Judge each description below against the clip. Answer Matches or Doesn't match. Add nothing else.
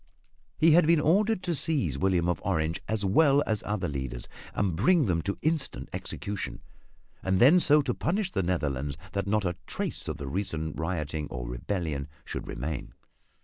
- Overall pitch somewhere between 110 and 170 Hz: Doesn't match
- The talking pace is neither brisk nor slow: Matches